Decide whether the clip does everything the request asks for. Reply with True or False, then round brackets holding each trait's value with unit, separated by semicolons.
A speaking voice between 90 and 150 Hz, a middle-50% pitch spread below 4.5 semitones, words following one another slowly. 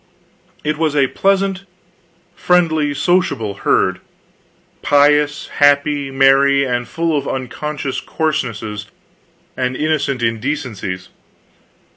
True (140 Hz; 3.2 semitones; 90 wpm)